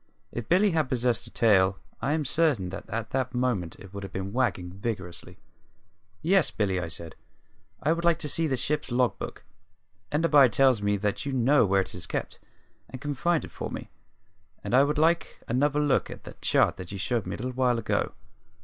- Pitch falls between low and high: No, low, 125 Hz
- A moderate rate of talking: No, fast, 210 wpm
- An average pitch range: No, wide, 6.7 semitones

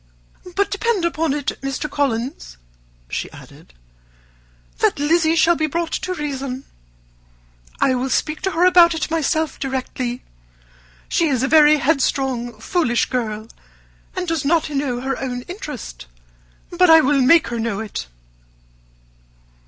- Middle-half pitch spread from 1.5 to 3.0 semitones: No, average, 4.6 semitones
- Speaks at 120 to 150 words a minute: Yes, slow, 135 wpm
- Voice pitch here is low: No, very high, 285 Hz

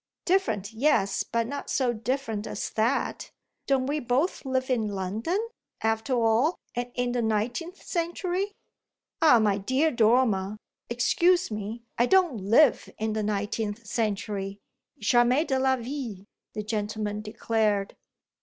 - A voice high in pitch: Yes, high, 235 Hz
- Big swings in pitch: No, average, 4.0 semitones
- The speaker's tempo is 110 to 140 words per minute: Yes, slow, 135 wpm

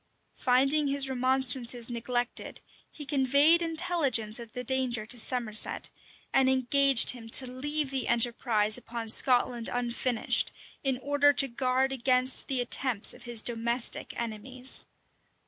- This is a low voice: No, very high, 255 Hz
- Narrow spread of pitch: Yes, narrow, 2.2 semitones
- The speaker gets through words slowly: Yes, slow, 130 wpm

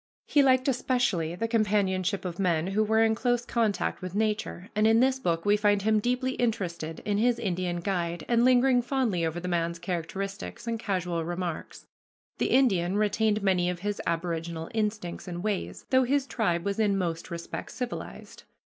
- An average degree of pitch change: Yes, average, 4.6 semitones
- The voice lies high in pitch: Yes, high, 200 Hz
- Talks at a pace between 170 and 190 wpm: Yes, average, 175 wpm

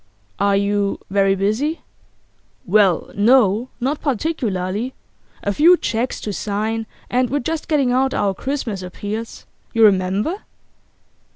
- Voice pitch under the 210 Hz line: No, high, 220 Hz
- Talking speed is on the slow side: Yes, slow, 120 wpm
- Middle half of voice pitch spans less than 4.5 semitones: No, average, 4.8 semitones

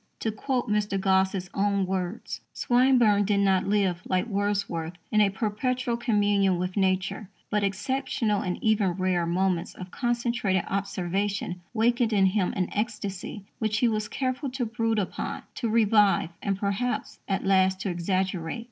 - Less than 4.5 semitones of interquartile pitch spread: Yes, average, 2.8 semitones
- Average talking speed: Yes, average, 150 wpm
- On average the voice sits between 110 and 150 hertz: No, high, 200 Hz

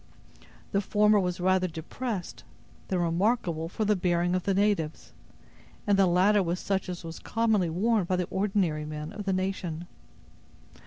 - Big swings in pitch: No, average, 2.9 semitones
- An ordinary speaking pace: Yes, average, 160 wpm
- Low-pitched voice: No, medium, 185 Hz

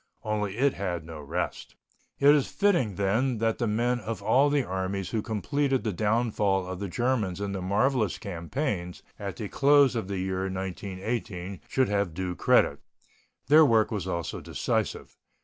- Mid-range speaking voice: No, low, 105 Hz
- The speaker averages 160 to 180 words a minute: Yes, average, 165 wpm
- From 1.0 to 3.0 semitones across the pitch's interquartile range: No, average, 4.7 semitones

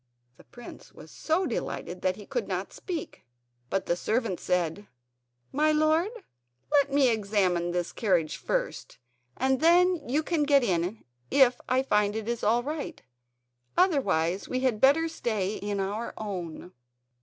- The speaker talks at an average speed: Yes, average, 150 wpm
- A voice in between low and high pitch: No, high, 230 Hz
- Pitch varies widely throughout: Yes, wide, 7.1 semitones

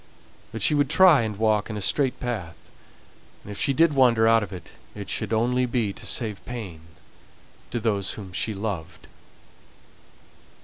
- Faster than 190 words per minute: No, average, 170 wpm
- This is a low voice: Yes, low, 110 Hz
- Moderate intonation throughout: Yes, average, 3.7 semitones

